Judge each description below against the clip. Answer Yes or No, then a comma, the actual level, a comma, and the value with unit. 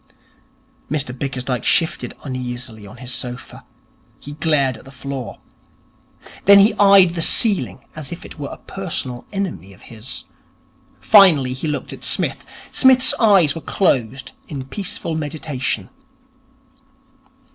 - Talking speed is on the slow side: Yes, slow, 130 wpm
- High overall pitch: No, medium, 140 Hz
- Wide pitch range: Yes, wide, 5.9 semitones